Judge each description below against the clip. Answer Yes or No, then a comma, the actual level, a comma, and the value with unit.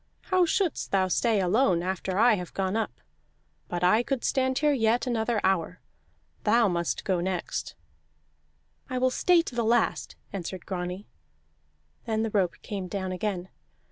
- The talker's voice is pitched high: Yes, high, 210 Hz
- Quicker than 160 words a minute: No, average, 155 wpm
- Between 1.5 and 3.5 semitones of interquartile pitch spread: No, average, 4.6 semitones